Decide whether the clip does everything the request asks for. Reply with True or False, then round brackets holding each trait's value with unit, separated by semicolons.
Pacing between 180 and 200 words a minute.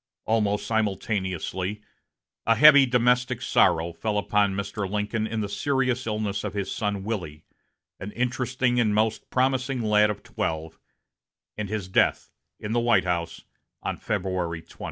False (145 wpm)